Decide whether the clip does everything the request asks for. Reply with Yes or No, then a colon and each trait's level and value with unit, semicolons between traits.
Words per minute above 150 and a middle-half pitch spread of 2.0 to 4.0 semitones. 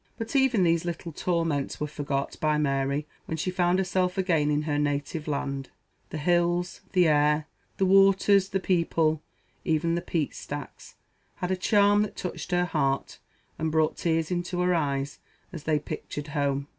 Yes: average, 170 wpm; average, 3.5 semitones